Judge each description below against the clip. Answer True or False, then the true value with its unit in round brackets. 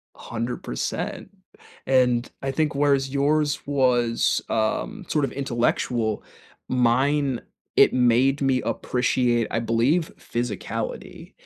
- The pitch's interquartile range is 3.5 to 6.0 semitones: False (2.8 semitones)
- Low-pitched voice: True (125 Hz)